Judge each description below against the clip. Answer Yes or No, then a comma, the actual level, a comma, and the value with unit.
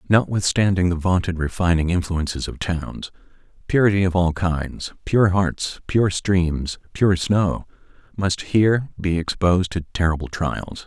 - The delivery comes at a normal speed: No, slow, 120 wpm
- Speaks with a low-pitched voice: Yes, very low, 90 Hz